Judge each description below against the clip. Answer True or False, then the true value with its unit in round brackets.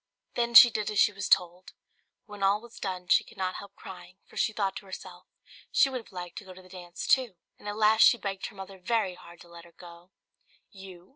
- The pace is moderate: False (245 wpm)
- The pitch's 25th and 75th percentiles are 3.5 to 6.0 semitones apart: False (2.8 semitones)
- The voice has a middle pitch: False (195 Hz)